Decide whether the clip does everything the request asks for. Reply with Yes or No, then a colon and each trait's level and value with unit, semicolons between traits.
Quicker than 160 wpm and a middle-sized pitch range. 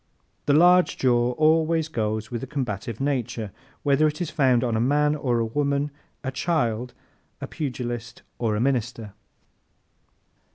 No: average, 150 wpm; average, 4.0 semitones